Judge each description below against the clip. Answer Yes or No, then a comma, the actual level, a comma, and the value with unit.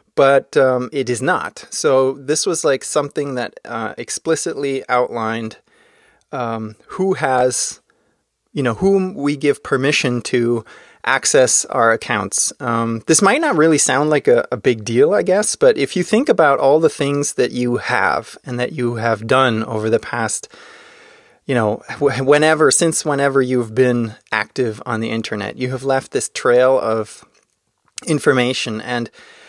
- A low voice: Yes, low, 130 Hz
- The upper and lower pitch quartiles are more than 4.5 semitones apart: No, average, 4.2 semitones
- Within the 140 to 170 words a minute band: Yes, average, 160 wpm